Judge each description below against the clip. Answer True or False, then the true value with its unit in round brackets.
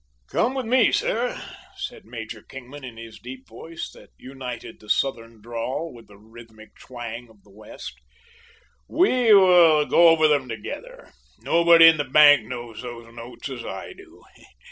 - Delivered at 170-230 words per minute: False (160 wpm)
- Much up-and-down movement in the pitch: True (6.2 semitones)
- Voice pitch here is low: True (125 Hz)